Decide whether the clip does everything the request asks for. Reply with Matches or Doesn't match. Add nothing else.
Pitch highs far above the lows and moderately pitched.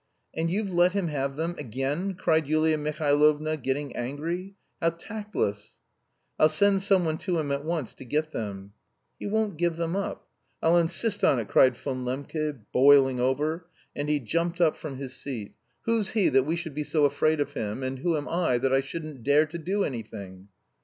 Doesn't match